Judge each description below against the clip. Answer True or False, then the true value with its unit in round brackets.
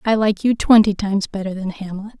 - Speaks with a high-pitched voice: True (205 Hz)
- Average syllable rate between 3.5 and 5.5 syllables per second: False (5.8 syllables/s)